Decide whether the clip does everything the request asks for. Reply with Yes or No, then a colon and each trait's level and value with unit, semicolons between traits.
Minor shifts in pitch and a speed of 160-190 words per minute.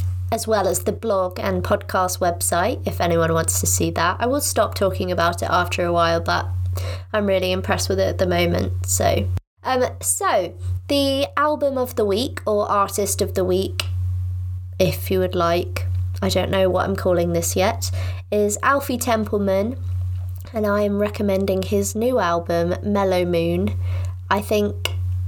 Yes: narrow, 2.2 semitones; average, 165 wpm